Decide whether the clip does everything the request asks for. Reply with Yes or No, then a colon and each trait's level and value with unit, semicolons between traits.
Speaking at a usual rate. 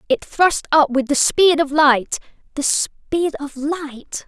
Yes: average, 155 wpm